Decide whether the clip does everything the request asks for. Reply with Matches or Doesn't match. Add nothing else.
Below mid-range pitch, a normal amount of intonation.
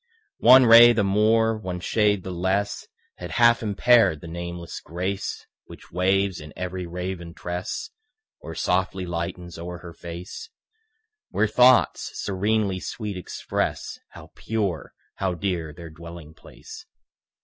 Matches